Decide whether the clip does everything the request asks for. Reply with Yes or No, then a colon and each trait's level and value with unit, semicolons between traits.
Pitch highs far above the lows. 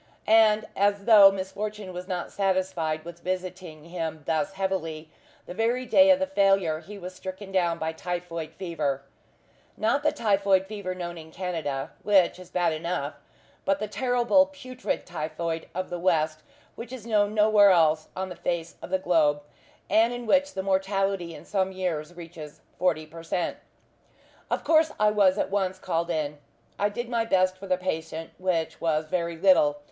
No: average, 3.6 semitones